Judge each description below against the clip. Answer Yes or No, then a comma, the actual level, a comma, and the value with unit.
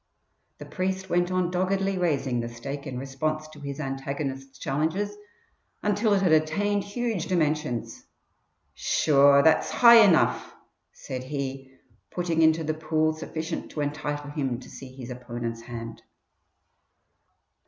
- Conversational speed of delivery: No, slow, 130 wpm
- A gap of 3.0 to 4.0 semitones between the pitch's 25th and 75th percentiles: No, average, 4.8 semitones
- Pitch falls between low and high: Yes, medium, 155 Hz